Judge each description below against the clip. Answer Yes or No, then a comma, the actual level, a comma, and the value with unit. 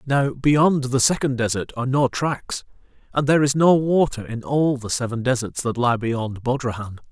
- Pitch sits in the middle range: No, low, 130 Hz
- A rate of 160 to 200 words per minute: Yes, average, 185 wpm